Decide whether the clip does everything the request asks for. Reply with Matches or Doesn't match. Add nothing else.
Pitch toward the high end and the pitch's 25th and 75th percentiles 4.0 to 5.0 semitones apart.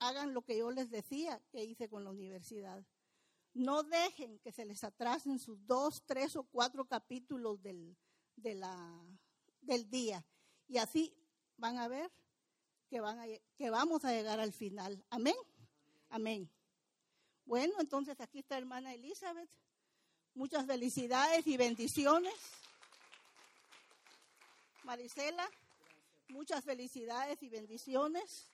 Matches